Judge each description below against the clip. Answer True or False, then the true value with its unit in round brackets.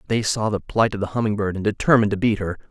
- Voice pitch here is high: False (105 Hz)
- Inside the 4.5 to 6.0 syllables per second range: False (7.1 syllables/s)